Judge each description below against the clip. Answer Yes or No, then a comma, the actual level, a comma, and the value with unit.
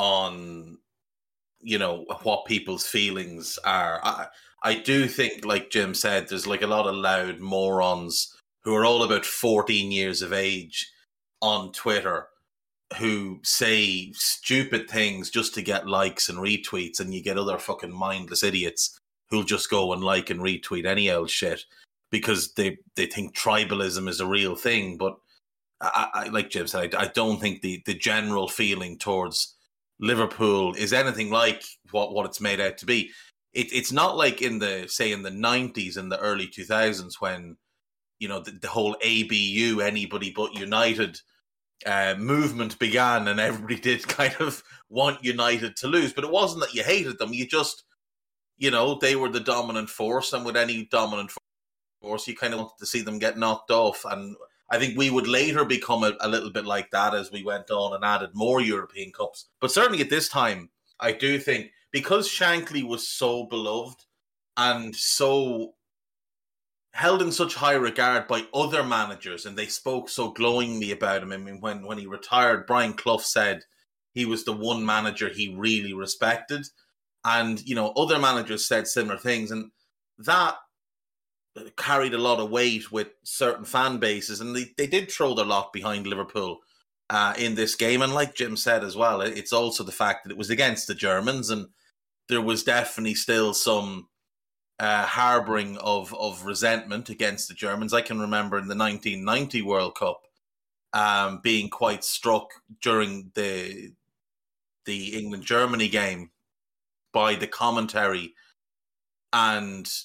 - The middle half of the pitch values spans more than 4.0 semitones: No, average, 3.1 semitones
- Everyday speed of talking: Yes, average, 170 wpm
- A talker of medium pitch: No, low, 110 Hz